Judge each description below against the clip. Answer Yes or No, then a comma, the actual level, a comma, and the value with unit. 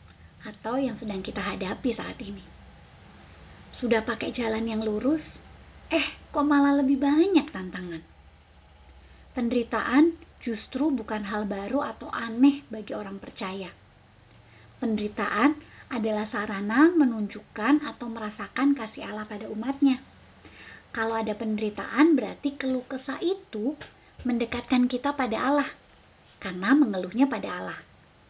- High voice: Yes, high, 230 Hz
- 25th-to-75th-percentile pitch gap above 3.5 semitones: Yes, average, 5.2 semitones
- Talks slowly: No, average, 110 wpm